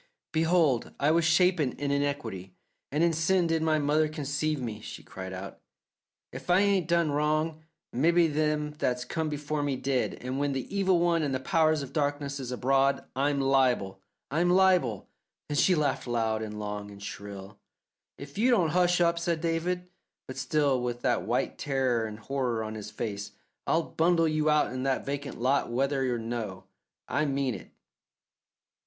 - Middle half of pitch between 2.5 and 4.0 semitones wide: No, average, 4.6 semitones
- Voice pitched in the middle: Yes, medium, 145 Hz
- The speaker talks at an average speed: Yes, average, 180 wpm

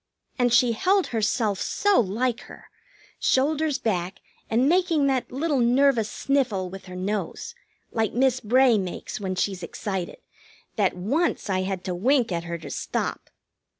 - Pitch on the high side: Yes, high, 230 Hz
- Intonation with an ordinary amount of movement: No, wide, 5.9 semitones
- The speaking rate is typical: Yes, average, 150 wpm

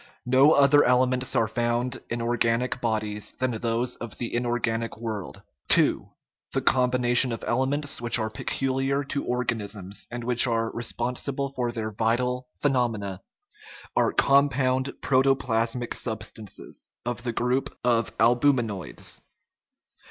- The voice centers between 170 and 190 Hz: No, low, 120 Hz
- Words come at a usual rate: No, slow, 130 wpm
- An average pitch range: No, narrow, 2.1 semitones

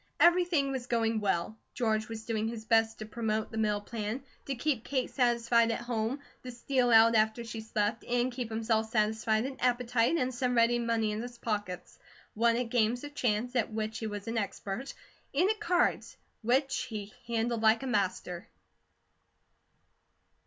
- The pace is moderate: Yes, average, 175 wpm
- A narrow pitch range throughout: Yes, narrow, 2.2 semitones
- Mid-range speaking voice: No, high, 230 Hz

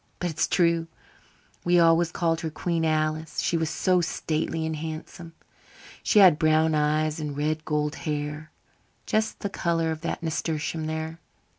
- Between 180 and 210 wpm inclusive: No, average, 160 wpm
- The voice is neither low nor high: Yes, medium, 160 Hz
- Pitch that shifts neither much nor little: No, narrow, 1.4 semitones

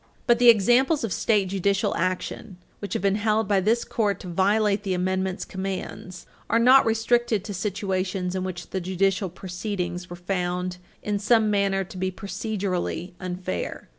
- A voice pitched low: No, high, 195 Hz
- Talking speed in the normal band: Yes, average, 165 wpm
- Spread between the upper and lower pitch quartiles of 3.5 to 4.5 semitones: No, narrow, 2.6 semitones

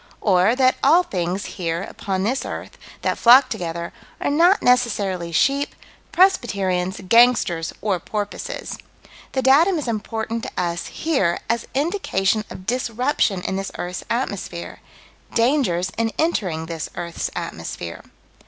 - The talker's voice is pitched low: No, high, 215 Hz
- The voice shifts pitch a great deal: Yes, wide, 6.3 semitones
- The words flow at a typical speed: No, slow, 130 wpm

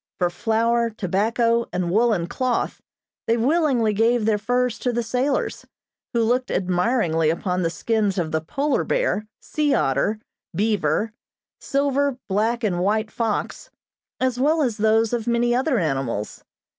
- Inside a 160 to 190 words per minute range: No, average, 145 wpm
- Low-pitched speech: No, high, 225 Hz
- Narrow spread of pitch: No, average, 4.3 semitones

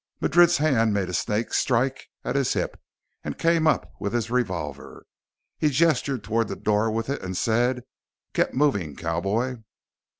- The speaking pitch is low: Yes, low, 115 Hz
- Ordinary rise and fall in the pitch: Yes, average, 4.9 semitones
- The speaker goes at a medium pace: Yes, average, 160 wpm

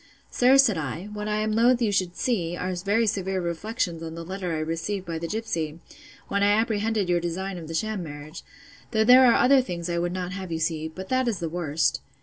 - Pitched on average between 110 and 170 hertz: No, medium, 185 Hz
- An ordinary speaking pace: No, fast, 230 wpm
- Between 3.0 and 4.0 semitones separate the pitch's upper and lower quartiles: No, average, 4.5 semitones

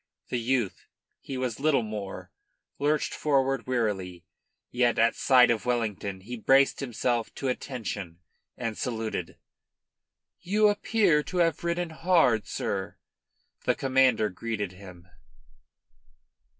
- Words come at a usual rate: No, slow, 115 wpm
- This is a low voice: Yes, low, 125 Hz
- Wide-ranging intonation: No, average, 4.5 semitones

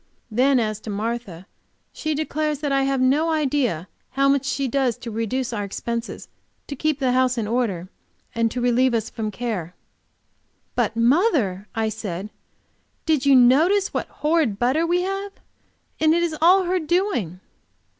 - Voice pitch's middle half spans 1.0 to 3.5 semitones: No, wide, 5.5 semitones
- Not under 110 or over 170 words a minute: Yes, average, 165 wpm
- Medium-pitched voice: No, very high, 255 Hz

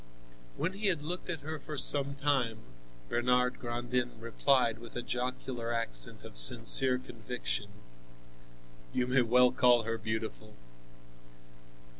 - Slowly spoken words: Yes, slow, 125 wpm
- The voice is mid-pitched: No, low, 125 Hz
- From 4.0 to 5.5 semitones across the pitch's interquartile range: No, average, 3.0 semitones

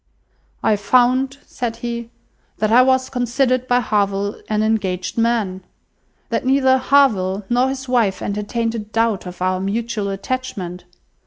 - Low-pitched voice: No, high, 230 Hz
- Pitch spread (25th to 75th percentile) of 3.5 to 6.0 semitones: Yes, average, 4.2 semitones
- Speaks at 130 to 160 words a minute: Yes, average, 140 wpm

